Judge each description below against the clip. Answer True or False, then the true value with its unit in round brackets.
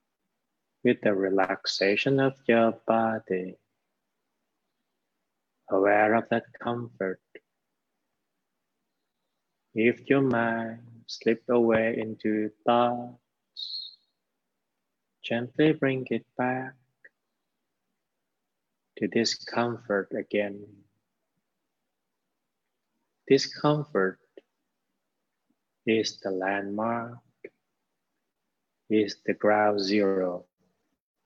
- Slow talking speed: True (65 wpm)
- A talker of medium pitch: False (115 Hz)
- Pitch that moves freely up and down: False (3.1 semitones)